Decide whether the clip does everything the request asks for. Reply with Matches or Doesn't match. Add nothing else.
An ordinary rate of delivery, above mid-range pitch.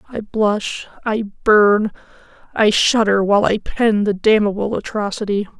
Doesn't match